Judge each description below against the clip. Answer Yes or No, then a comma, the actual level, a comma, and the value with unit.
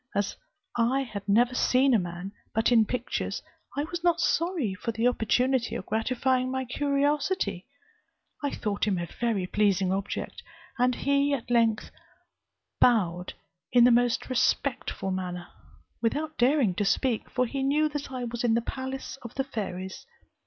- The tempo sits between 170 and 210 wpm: No, average, 160 wpm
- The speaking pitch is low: No, high, 240 Hz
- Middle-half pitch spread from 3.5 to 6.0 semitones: Yes, average, 4.6 semitones